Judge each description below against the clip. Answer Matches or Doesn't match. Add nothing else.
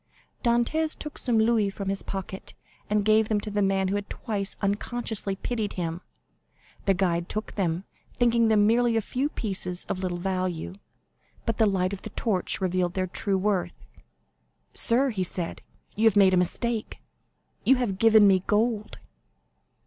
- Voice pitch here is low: Doesn't match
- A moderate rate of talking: Matches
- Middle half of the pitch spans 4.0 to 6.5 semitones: Doesn't match